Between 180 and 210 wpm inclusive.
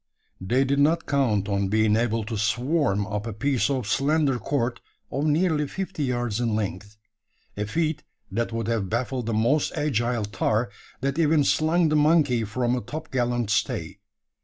No: average, 165 wpm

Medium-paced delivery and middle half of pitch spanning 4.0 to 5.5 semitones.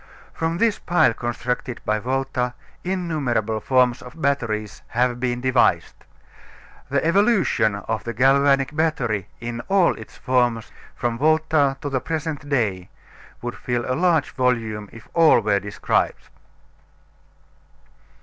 No: slow, 125 wpm; average, 4.6 semitones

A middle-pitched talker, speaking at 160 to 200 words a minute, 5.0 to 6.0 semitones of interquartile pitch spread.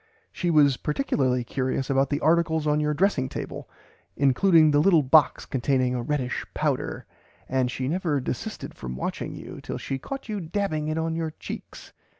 No: medium, 150 Hz; average, 170 wpm; average, 3.7 semitones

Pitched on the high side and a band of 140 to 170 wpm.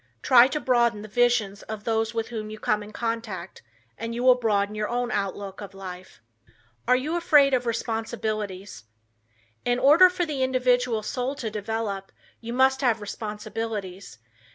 Yes: high, 225 Hz; average, 160 wpm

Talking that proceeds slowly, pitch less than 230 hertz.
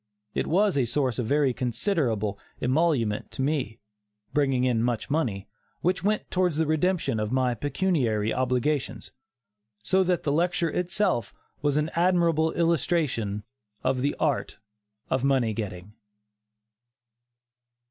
Yes: slow, 125 wpm; medium, 140 Hz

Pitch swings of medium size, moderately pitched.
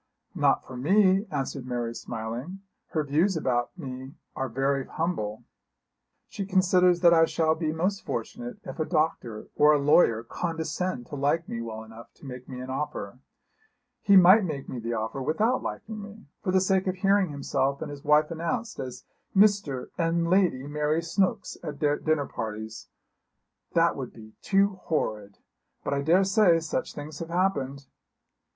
No: wide, 6.0 semitones; medium, 155 Hz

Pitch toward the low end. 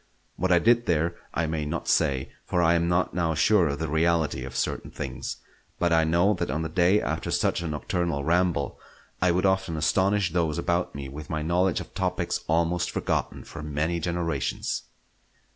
Yes: very low, 85 Hz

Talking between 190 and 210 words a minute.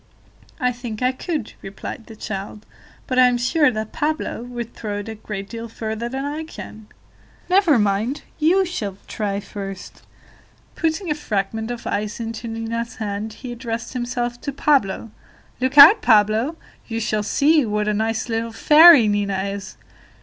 No: average, 165 wpm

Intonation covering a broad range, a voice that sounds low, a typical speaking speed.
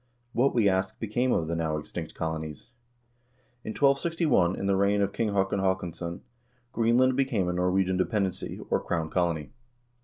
No: average, 4.9 semitones; very low, 95 Hz; average, 155 wpm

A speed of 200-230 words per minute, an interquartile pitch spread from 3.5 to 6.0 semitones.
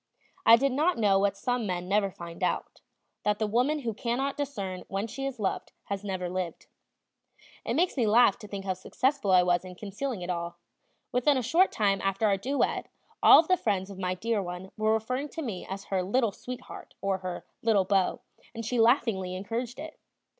Yes: fast, 205 wpm; average, 4.7 semitones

